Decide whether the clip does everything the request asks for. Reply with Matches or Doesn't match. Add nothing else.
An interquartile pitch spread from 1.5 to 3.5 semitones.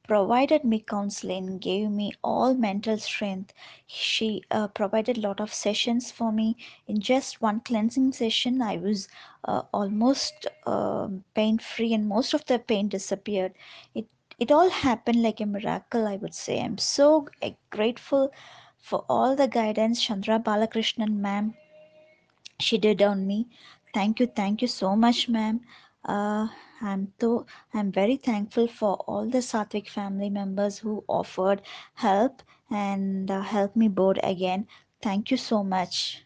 Matches